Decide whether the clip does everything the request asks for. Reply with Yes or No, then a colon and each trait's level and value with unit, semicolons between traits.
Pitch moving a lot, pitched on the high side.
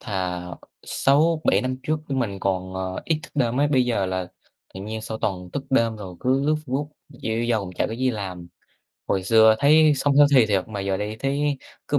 No: wide, 6.2 semitones; low, 115 Hz